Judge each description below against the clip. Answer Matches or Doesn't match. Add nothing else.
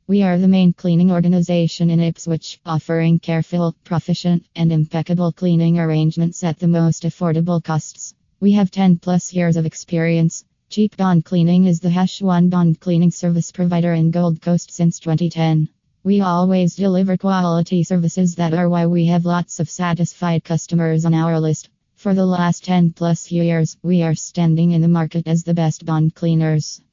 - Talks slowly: Doesn't match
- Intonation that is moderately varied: Doesn't match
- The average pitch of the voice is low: Doesn't match